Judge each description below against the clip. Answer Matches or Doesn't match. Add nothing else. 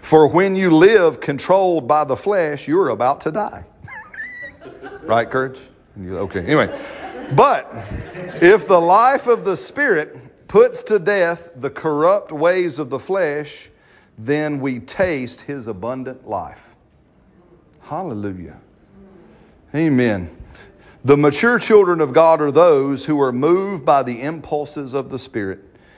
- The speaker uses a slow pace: Matches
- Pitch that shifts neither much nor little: Doesn't match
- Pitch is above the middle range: Doesn't match